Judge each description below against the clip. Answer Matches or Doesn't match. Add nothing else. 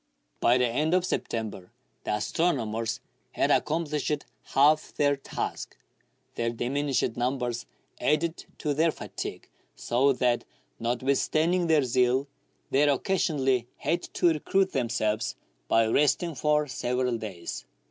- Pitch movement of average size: Matches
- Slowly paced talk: Matches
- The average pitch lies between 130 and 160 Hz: Matches